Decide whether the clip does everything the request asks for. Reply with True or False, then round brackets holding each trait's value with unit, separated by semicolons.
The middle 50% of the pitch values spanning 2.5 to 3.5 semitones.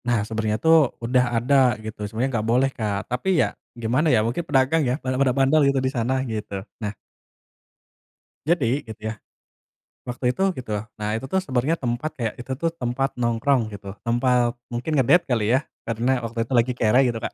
True (2.8 semitones)